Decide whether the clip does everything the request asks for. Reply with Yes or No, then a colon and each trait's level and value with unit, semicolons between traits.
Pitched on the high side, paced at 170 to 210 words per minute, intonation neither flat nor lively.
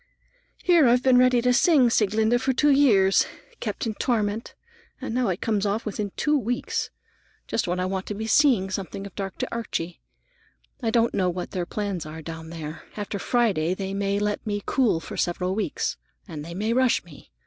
Yes: high, 205 Hz; average, 190 wpm; average, 4.5 semitones